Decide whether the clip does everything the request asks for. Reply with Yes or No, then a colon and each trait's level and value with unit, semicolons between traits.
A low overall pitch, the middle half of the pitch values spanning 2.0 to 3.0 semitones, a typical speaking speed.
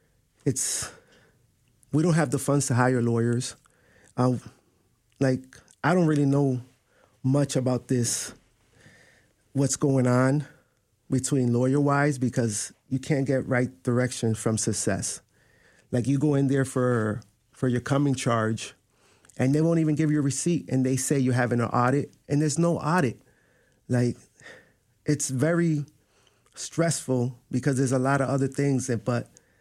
Yes: low, 130 Hz; average, 2.7 semitones; average, 150 wpm